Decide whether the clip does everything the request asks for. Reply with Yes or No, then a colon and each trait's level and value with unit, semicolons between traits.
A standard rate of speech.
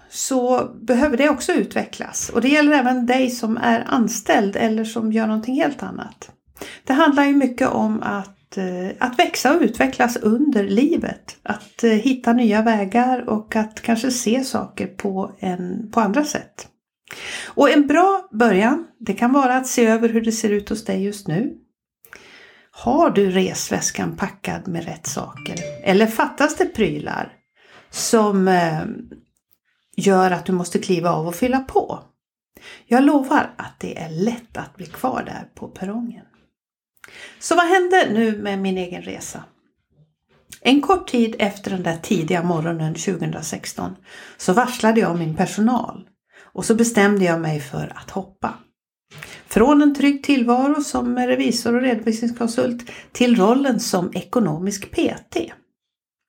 Yes: average, 150 wpm